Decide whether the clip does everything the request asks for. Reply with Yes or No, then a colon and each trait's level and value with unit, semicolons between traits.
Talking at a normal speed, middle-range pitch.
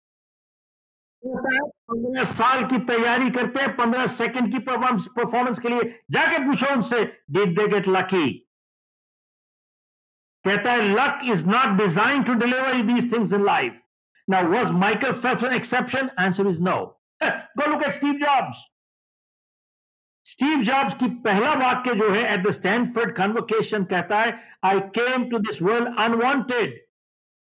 No: average, 140 wpm; high, 240 Hz